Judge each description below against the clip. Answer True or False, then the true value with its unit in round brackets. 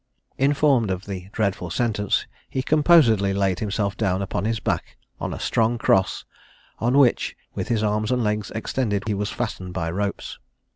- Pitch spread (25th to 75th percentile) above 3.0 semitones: True (3.4 semitones)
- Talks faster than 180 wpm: False (165 wpm)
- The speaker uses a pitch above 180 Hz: False (105 Hz)